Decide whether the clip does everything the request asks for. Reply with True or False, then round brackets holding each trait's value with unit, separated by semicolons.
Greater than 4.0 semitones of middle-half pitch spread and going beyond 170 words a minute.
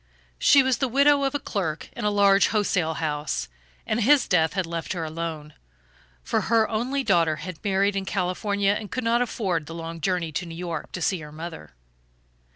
True (4.9 semitones; 195 wpm)